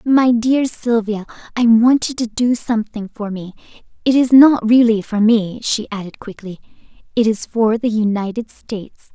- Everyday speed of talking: Yes, average, 170 wpm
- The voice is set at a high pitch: Yes, high, 225 Hz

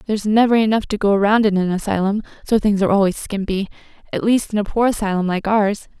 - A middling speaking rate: No, fast, 220 wpm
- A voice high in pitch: Yes, high, 205 Hz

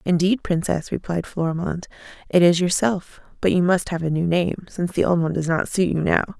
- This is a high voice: No, medium, 175 Hz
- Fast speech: Yes, fast, 215 wpm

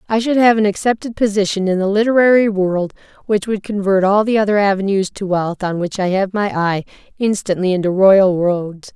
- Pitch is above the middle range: Yes, high, 200 Hz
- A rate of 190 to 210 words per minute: Yes, average, 195 wpm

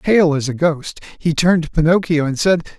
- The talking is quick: Yes, fast, 215 wpm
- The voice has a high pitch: No, medium, 160 Hz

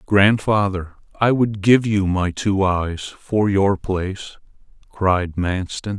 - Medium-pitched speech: No, low, 100 Hz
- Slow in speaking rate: Yes, slow, 130 wpm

